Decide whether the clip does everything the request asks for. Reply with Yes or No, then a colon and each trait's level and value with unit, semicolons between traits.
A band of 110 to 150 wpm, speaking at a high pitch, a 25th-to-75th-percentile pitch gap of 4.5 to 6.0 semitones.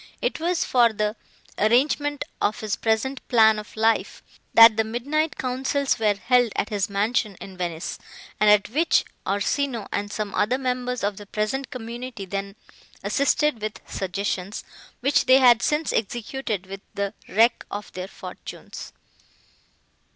No: average, 145 wpm; high, 225 Hz; average, 3.9 semitones